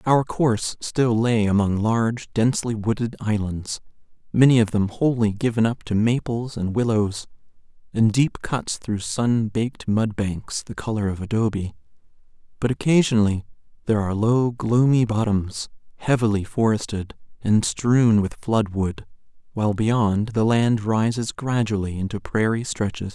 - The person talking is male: Yes, male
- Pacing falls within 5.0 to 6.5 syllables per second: No, 4.6 syllables/s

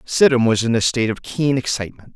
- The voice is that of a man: Yes, male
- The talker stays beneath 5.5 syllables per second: No, 6.3 syllables/s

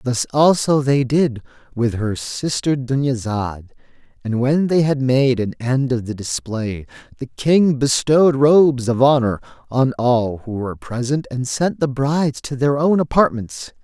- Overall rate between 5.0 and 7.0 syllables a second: No, 4.3 syllables/s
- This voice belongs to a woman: No, male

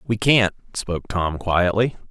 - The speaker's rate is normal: Yes, average, 145 wpm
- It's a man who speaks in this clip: Yes, male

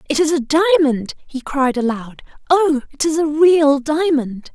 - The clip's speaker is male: No, female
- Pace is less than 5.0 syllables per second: Yes, 4.1 syllables/s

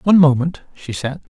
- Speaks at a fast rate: No, average, 180 wpm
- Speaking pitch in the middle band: Yes, medium, 145 Hz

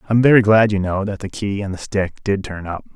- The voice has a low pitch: Yes, low, 100 Hz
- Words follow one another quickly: Yes, fast, 285 wpm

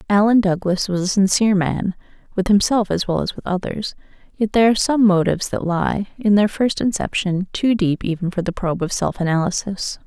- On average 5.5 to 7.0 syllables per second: Yes, 5.6 syllables/s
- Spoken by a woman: Yes, female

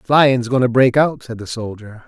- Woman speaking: No, male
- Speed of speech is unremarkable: No, fast, 230 wpm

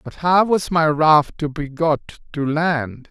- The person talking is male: Yes, male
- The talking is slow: No, average, 195 wpm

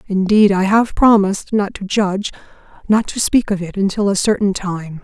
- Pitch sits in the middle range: No, high, 200 Hz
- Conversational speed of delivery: Yes, average, 190 wpm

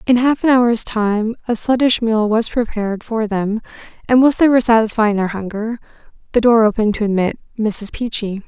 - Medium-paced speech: Yes, average, 185 wpm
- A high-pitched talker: Yes, high, 225 Hz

